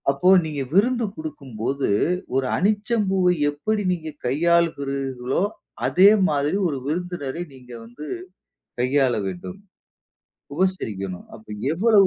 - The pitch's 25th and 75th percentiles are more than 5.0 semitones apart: Yes, wide, 5.5 semitones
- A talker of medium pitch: Yes, medium, 150 Hz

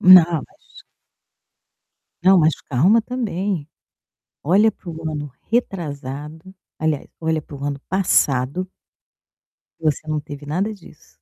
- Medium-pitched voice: Yes, medium, 160 Hz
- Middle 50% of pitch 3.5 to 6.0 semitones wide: Yes, average, 4.4 semitones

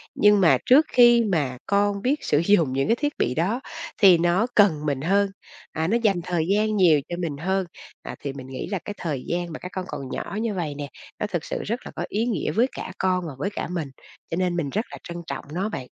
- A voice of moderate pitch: Yes, medium, 180 Hz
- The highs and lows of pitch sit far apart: No, average, 4.7 semitones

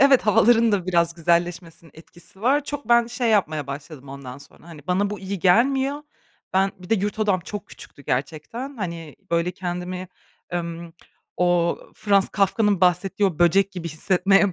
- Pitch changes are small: No, average, 3.6 semitones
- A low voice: No, medium, 185 Hz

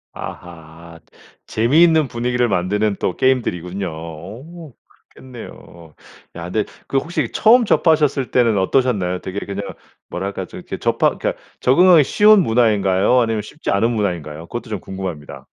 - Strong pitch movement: Yes, wide, 6.3 semitones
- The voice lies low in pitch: Yes, low, 110 Hz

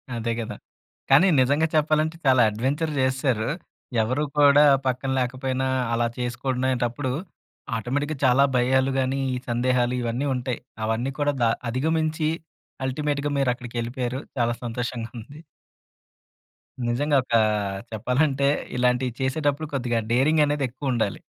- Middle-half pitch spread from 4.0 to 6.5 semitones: No, average, 2.8 semitones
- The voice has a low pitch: Yes, low, 130 Hz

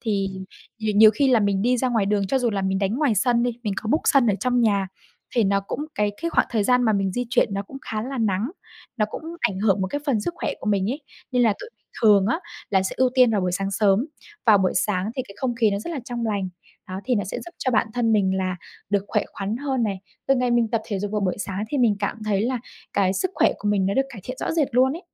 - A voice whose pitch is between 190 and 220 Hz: Yes, high, 215 Hz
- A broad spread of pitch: No, average, 3.9 semitones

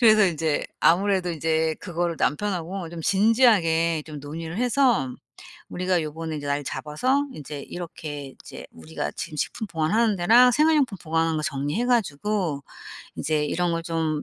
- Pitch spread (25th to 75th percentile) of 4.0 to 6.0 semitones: Yes, average, 5.1 semitones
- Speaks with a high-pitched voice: No, medium, 165 Hz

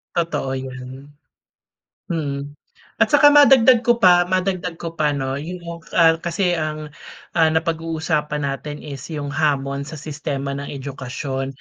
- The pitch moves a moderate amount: Yes, average, 3.6 semitones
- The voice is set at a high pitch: No, medium, 155 Hz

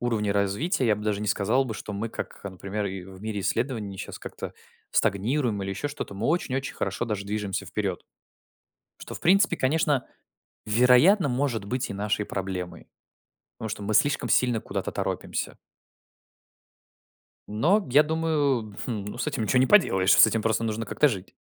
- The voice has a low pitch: Yes, low, 110 Hz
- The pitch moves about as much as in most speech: Yes, average, 4.7 semitones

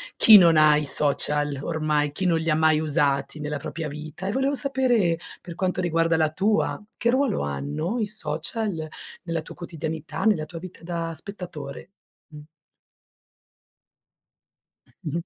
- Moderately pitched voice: Yes, medium, 165 Hz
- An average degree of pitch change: Yes, average, 3.7 semitones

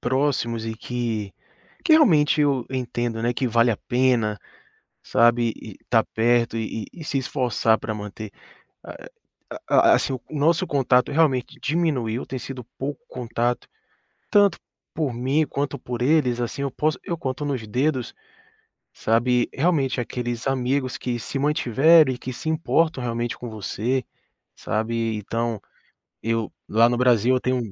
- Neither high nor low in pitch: No, low, 125 Hz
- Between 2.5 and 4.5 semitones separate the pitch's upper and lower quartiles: Yes, average, 3.4 semitones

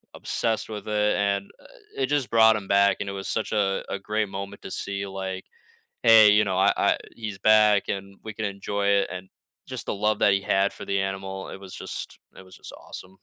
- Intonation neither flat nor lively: No, narrow, 1.7 semitones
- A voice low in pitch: Yes, low, 100 Hz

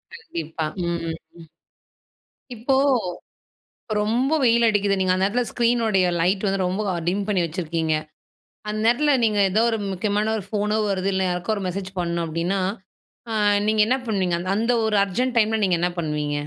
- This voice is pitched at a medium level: No, high, 195 Hz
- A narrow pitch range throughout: No, average, 3.8 semitones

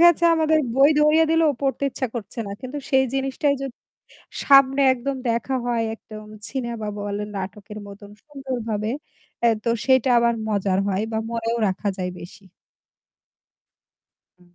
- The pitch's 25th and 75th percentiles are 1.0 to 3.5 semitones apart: No, average, 4.6 semitones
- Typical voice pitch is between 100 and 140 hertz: No, high, 235 Hz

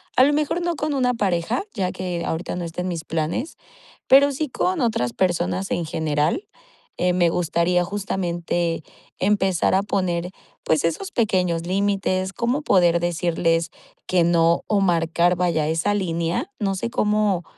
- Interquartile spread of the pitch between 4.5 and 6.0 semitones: No, average, 3.5 semitones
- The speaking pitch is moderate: Yes, medium, 180 Hz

